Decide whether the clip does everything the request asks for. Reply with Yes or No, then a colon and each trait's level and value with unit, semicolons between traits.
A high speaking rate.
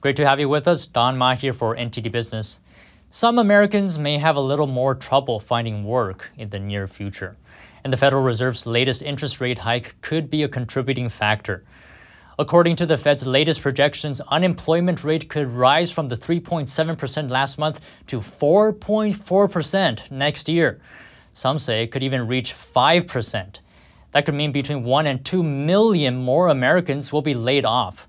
No: average, 170 wpm